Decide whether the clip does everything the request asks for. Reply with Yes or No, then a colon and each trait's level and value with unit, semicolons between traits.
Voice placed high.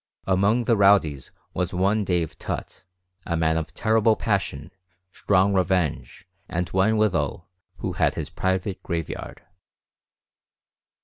No: very low, 95 Hz